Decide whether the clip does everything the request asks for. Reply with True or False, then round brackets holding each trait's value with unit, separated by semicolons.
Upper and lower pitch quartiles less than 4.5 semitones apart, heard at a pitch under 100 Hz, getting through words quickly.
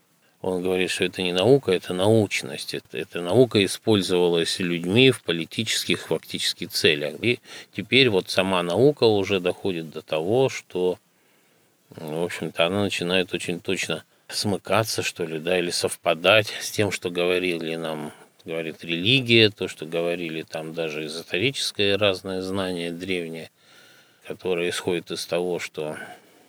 False (2.8 semitones; 90 Hz; 140 wpm)